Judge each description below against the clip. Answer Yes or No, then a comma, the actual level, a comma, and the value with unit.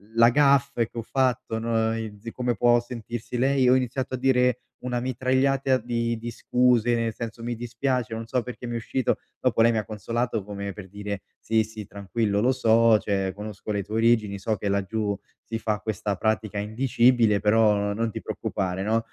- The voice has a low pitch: Yes, low, 115 Hz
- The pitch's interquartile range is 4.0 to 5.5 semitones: No, narrow, 2.6 semitones